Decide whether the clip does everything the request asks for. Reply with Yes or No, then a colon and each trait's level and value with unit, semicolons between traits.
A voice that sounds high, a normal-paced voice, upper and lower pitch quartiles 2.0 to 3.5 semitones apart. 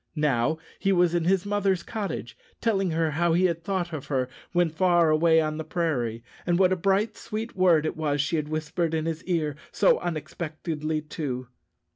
No: medium, 165 Hz; average, 190 wpm; average, 2.9 semitones